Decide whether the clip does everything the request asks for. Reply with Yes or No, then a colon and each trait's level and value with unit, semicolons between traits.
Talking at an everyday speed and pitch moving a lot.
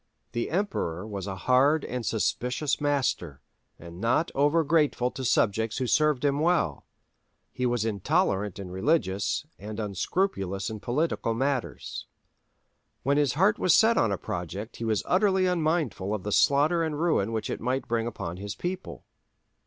Yes: average, 160 wpm; wide, 7.1 semitones